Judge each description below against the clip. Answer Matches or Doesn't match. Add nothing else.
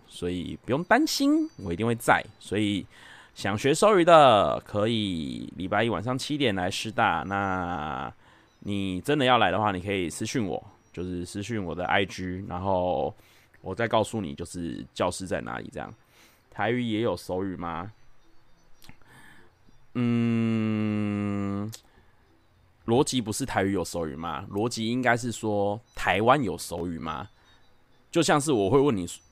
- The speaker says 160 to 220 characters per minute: Matches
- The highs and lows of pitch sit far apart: Doesn't match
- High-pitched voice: Doesn't match